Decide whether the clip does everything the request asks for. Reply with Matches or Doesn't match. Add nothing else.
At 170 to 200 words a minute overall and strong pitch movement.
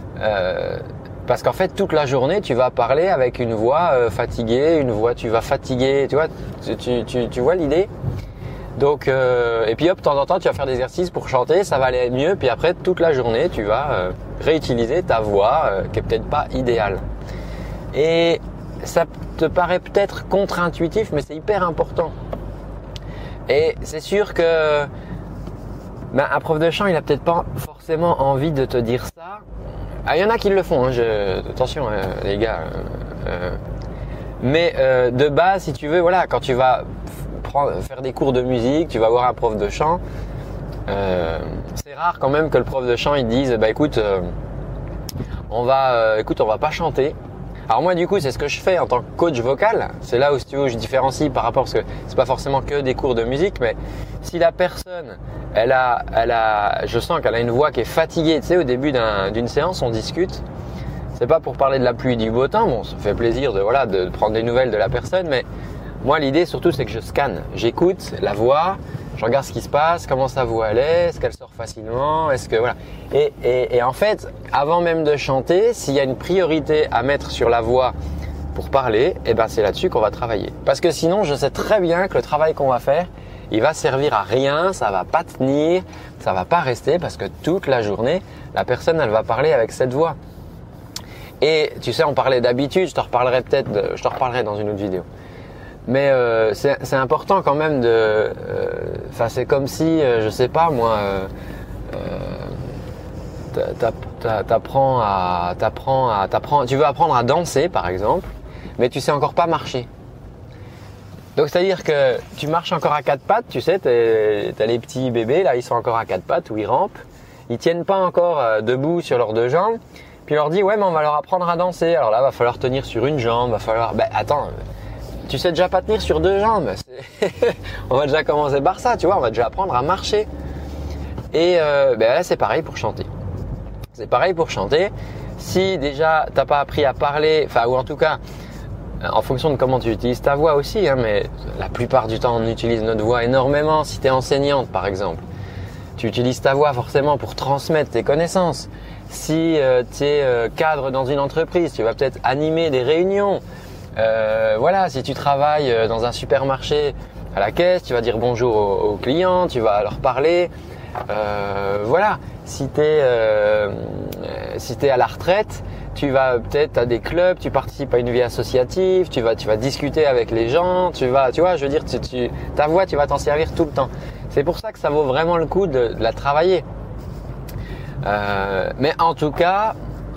Doesn't match